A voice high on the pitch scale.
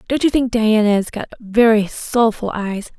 Yes: high, 220 Hz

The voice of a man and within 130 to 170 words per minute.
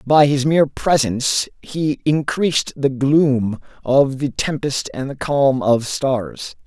Yes: male; average, 145 wpm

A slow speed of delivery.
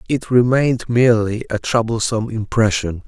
Yes: slow, 115 wpm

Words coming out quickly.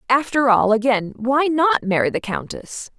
No: average, 160 wpm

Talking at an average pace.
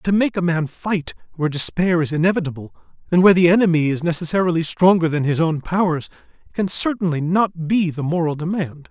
Yes: average, 180 wpm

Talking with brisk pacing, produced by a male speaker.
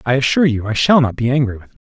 Yes: fast, 320 wpm; male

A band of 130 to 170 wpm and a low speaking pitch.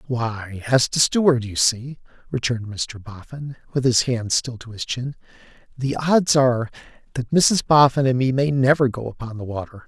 No: average, 180 wpm; low, 125 Hz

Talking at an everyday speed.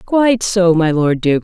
No: fast, 210 wpm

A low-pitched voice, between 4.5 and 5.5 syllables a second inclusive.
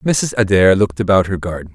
No: low, 100 Hz; 6.0 syllables/s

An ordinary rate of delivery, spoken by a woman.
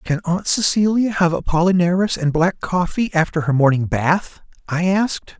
No: average, 155 wpm; male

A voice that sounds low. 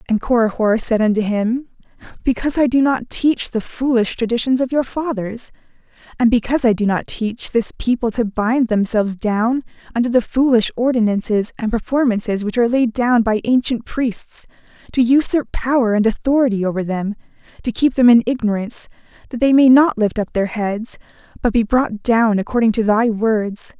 No: high, 230 Hz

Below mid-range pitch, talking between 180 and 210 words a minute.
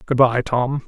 Yes: low, 125 Hz; fast, 205 wpm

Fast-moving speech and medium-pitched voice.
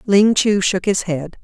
No: fast, 210 wpm; high, 195 Hz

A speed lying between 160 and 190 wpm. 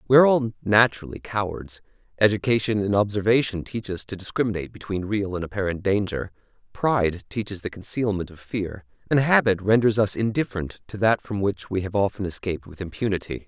Yes: average, 170 wpm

